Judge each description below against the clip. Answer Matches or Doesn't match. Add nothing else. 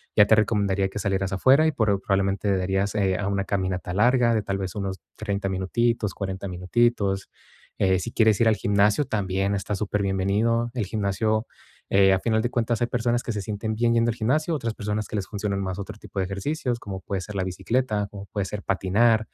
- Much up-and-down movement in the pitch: Doesn't match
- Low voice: Matches